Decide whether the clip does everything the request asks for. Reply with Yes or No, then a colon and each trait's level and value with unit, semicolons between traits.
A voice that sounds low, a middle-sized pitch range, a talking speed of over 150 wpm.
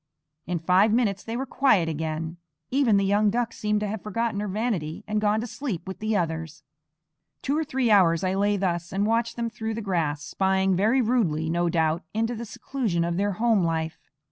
No: high, 200 Hz; average, 4.8 semitones; fast, 205 wpm